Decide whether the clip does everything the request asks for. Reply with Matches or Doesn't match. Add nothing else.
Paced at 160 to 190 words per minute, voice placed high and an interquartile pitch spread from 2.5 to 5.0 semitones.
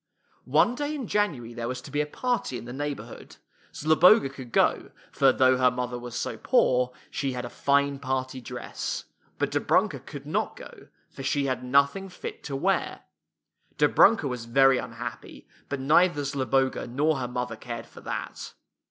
Doesn't match